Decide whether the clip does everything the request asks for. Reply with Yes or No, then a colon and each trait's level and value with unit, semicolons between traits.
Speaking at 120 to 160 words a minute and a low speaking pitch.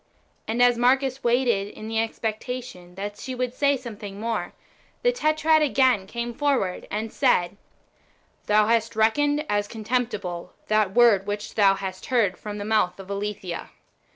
No: average, 155 wpm; high, 220 Hz